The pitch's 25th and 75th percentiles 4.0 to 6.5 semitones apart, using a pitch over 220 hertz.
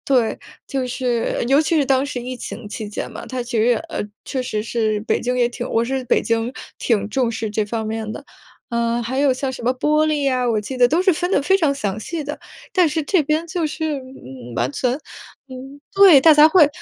Yes: average, 4.4 semitones; very high, 255 Hz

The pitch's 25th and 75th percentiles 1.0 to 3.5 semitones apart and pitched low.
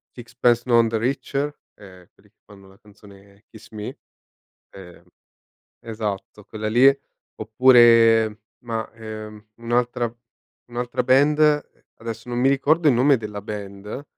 Yes: narrow, 2.6 semitones; low, 115 Hz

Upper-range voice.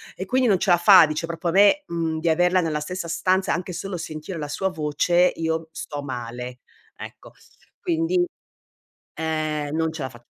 No: medium, 165 Hz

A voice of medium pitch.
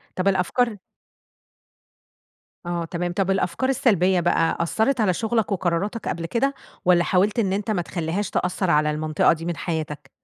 Yes: medium, 180 Hz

